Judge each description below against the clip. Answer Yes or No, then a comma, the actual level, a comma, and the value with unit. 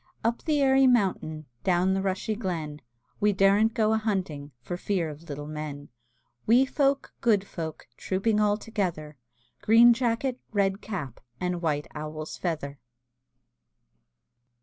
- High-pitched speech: Yes, high, 195 Hz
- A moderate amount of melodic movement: No, wide, 6.2 semitones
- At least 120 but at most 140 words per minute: Yes, slow, 135 wpm